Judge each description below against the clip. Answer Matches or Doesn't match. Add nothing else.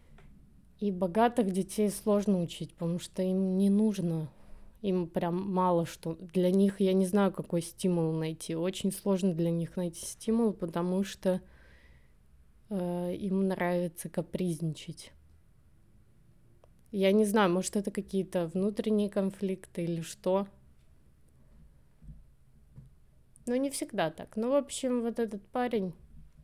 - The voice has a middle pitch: Matches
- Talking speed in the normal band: Matches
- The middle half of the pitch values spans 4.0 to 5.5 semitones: Doesn't match